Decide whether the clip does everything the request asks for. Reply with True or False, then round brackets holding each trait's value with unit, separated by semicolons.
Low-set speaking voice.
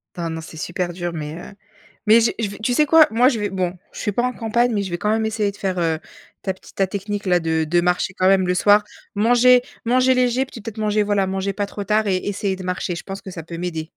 False (200 Hz)